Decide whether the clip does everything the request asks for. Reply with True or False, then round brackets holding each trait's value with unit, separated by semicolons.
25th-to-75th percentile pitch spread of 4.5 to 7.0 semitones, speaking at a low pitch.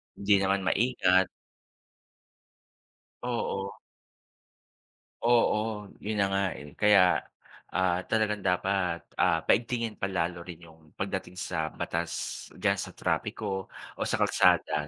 False (3.1 semitones; 95 Hz)